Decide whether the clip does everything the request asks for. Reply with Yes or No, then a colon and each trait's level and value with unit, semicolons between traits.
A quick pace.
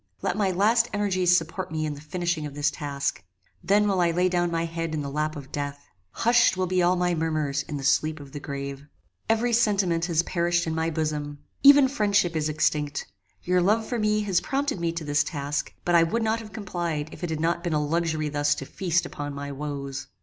Yes: fast, 225 wpm